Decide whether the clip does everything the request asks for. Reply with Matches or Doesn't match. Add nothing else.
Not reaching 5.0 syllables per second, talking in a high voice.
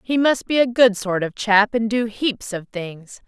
Matches